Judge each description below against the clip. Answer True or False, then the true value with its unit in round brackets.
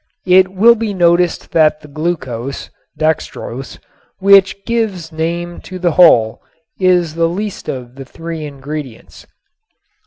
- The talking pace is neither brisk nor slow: False (125 wpm)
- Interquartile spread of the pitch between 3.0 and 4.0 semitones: True (3.6 semitones)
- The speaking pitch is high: False (170 Hz)